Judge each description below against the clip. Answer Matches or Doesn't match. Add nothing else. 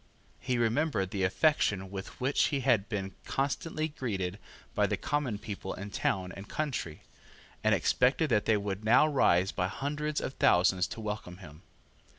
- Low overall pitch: Matches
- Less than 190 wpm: Matches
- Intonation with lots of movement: Matches